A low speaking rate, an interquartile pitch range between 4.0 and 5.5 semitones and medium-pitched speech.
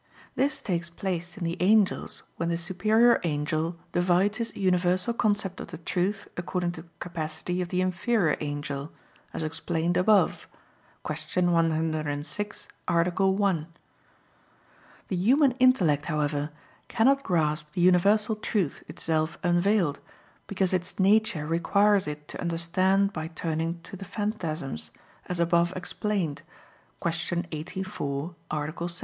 No: slow, 130 wpm; average, 3.4 semitones; medium, 175 Hz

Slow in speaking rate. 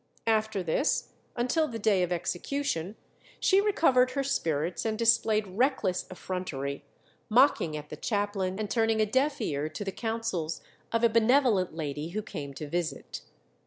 No: average, 155 wpm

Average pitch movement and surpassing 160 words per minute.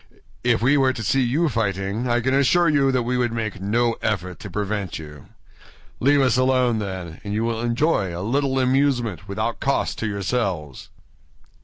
Yes: average, 4.5 semitones; average, 180 wpm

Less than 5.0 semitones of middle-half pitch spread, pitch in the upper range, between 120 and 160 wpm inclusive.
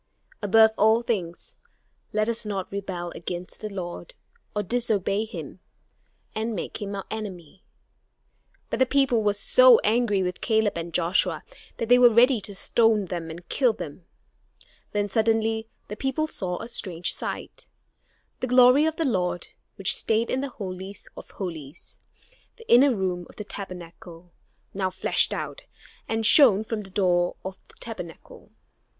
Yes: average, 4.2 semitones; high, 210 Hz; average, 155 wpm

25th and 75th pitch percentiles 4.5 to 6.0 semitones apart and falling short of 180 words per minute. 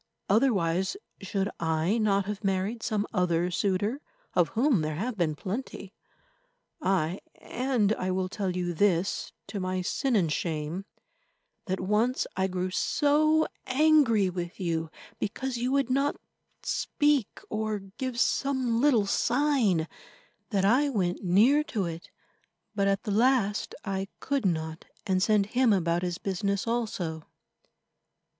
Yes: average, 5.0 semitones; slow, 135 wpm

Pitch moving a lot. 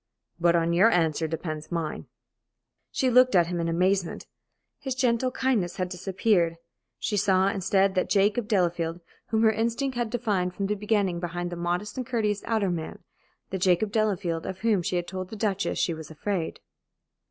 No: average, 3.9 semitones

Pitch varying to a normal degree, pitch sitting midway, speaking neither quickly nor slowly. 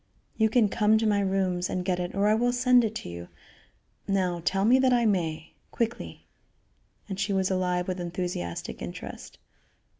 No: average, 3.6 semitones; high, 195 Hz; average, 180 wpm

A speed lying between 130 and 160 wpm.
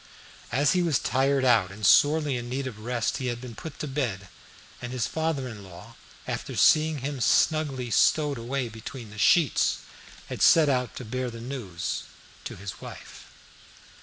No: average, 175 wpm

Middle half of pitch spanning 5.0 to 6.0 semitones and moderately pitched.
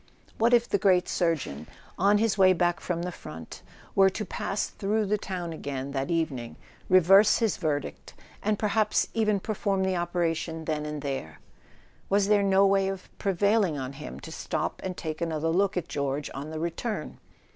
No: average, 4.2 semitones; medium, 180 Hz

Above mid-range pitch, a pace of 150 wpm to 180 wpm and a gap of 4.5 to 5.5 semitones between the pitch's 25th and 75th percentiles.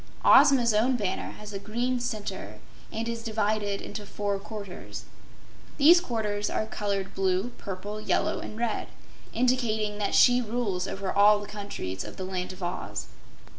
No: high, 210 Hz; average, 155 wpm; average, 2.7 semitones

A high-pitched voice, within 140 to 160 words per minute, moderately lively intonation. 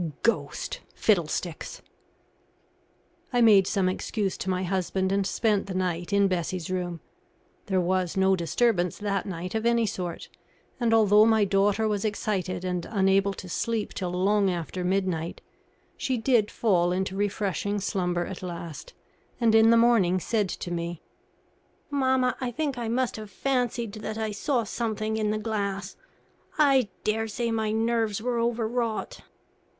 Yes: high, 205 Hz; average, 155 wpm; average, 3.4 semitones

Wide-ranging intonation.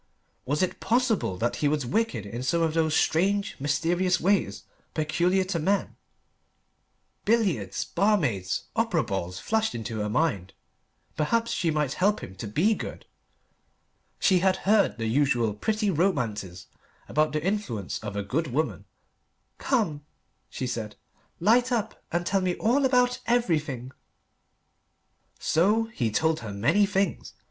Yes: wide, 9.0 semitones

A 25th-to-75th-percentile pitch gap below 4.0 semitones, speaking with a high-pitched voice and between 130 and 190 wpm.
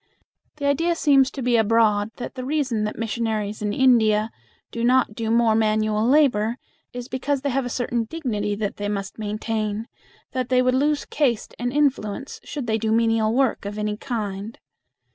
Yes: average, 3.4 semitones; high, 230 Hz; average, 180 wpm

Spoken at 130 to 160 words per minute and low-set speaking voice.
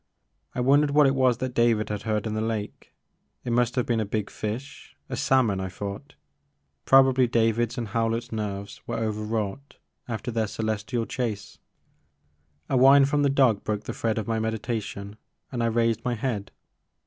No: average, 175 wpm; low, 115 Hz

